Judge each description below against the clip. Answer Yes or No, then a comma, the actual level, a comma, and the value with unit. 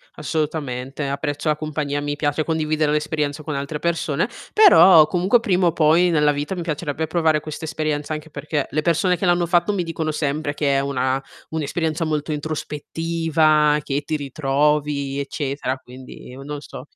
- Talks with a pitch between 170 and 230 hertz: No, medium, 150 Hz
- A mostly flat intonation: Yes, narrow, 2.0 semitones